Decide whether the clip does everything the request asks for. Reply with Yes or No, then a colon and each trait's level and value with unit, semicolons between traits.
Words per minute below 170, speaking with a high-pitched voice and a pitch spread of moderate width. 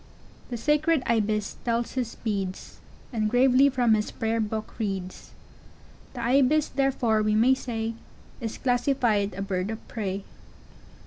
Yes: average, 140 wpm; high, 230 Hz; average, 3.1 semitones